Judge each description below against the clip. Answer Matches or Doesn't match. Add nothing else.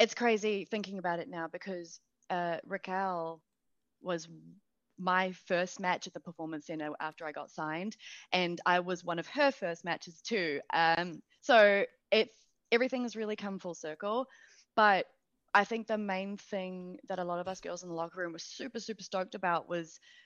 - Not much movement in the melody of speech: Doesn't match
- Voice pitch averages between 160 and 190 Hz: Matches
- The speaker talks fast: Doesn't match